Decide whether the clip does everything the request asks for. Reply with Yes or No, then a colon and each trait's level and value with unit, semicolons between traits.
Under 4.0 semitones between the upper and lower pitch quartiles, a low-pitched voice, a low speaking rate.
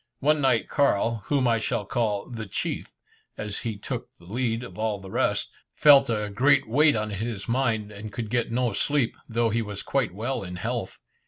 No: average, 3.2 semitones; low, 115 Hz; average, 195 wpm